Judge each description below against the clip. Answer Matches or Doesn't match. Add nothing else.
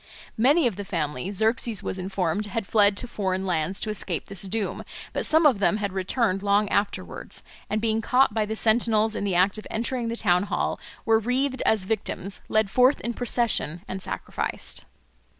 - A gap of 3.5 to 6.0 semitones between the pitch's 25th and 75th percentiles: Doesn't match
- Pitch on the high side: Matches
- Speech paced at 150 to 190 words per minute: Matches